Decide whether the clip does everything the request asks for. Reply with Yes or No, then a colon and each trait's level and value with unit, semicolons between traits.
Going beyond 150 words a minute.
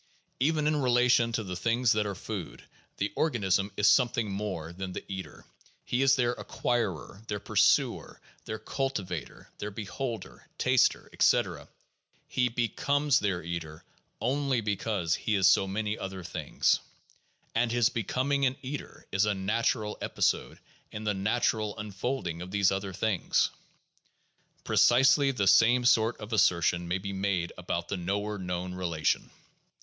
No: average, 145 wpm